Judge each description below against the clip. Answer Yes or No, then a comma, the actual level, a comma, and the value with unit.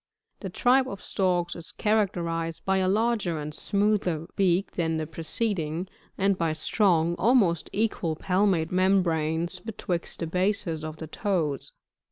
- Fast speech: No, average, 145 wpm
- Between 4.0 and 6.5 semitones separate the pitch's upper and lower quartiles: No, average, 3.6 semitones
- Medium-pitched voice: Yes, medium, 180 Hz